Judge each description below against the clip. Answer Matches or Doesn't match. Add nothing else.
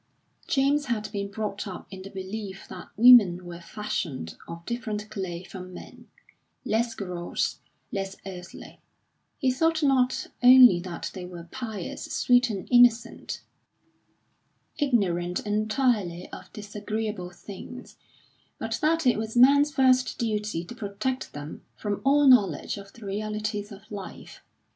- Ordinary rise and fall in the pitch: Matches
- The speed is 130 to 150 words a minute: Matches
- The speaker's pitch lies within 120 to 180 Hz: Doesn't match